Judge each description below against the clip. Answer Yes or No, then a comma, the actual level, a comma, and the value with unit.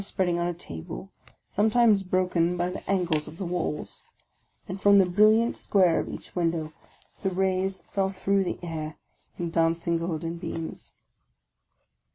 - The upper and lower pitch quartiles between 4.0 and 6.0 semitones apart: No, narrow, 2.6 semitones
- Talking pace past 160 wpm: Yes, average, 170 wpm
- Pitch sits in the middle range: Yes, medium, 180 Hz